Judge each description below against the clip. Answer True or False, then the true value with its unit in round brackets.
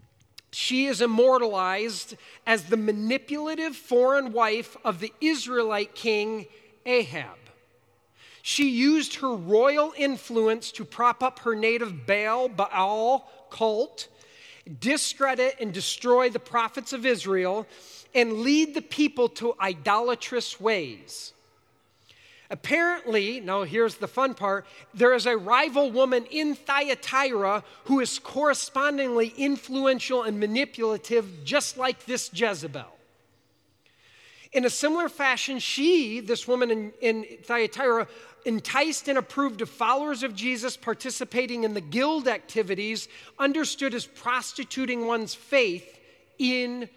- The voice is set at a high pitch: True (245 Hz)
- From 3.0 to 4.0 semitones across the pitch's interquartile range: True (3.5 semitones)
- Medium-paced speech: False (115 wpm)